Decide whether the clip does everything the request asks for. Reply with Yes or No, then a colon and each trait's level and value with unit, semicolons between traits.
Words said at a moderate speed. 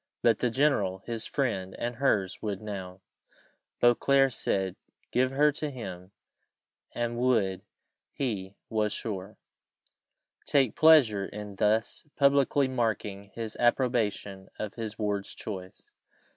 No: slow, 115 wpm